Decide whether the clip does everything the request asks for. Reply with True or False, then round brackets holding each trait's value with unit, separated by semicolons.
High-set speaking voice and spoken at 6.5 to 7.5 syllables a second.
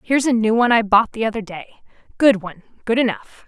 True (225 Hz; 6.6 syllables/s)